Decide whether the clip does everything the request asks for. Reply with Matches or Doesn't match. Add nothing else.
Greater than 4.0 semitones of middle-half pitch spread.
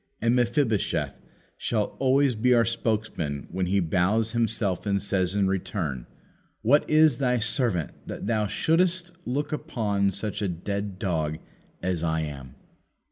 Matches